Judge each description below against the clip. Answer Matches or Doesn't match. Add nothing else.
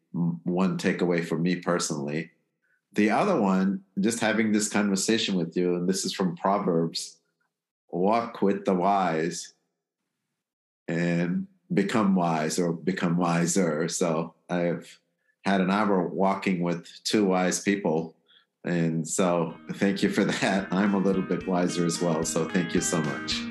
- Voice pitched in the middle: Doesn't match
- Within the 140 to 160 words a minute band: Matches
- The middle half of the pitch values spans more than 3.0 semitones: Doesn't match